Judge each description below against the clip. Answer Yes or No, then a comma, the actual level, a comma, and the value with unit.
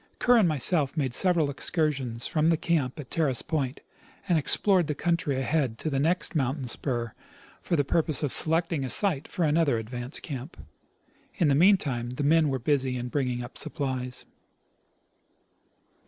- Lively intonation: No, average, 4.1 semitones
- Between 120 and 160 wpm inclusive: No, average, 170 wpm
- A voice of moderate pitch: Yes, medium, 145 Hz